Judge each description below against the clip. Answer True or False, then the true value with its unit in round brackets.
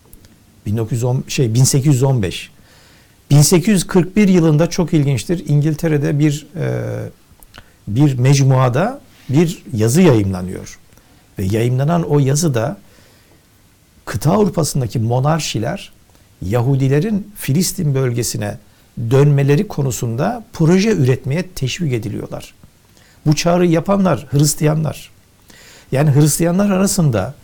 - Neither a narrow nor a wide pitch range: False (6.5 semitones)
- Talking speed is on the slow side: True (85 wpm)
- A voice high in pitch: False (140 Hz)